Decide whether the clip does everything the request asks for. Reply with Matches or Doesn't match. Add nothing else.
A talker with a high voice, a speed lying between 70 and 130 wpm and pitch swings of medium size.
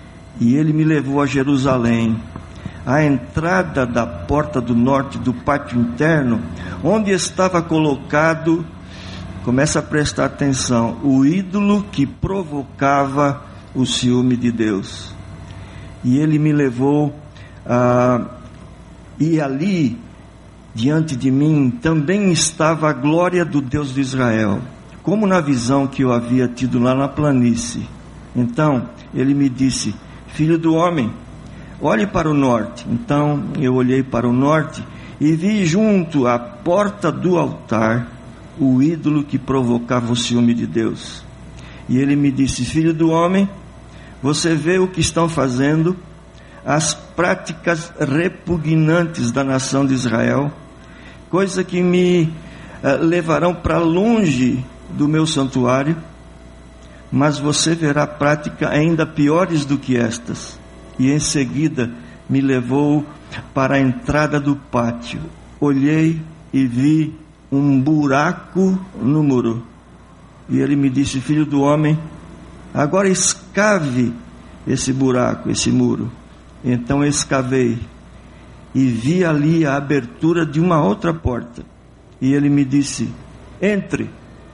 Doesn't match